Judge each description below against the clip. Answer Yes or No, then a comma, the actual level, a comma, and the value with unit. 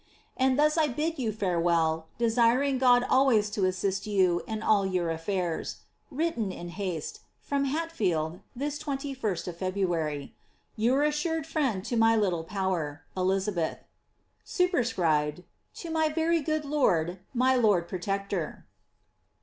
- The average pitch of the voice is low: No, high, 215 Hz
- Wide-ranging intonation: Yes, wide, 7.6 semitones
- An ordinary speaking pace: No, slow, 130 wpm